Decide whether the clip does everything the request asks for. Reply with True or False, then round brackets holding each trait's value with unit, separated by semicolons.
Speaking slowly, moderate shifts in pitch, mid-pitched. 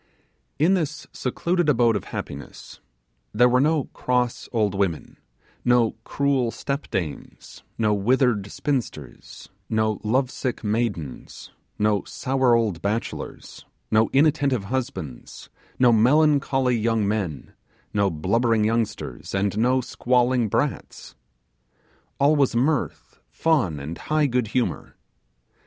False (110 wpm; 4.3 semitones; 120 Hz)